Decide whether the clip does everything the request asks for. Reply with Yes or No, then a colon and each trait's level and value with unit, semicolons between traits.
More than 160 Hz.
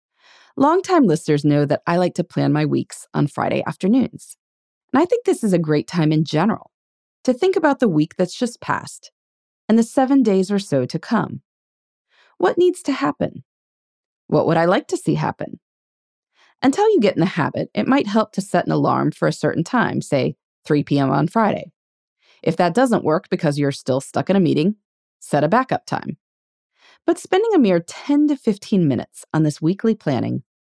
Yes: high, 190 Hz